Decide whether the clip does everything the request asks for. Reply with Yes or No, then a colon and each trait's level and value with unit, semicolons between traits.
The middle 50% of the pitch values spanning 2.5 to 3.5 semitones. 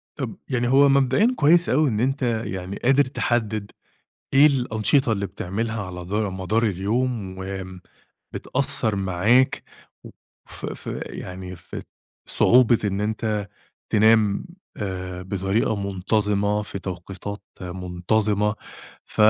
No: average, 4.0 semitones